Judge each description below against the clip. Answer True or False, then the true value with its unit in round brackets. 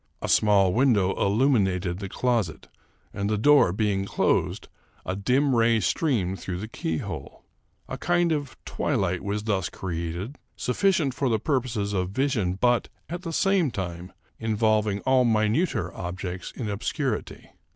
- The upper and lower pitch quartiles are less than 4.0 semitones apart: False (5.5 semitones)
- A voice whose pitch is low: True (110 Hz)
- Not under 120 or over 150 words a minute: True (140 wpm)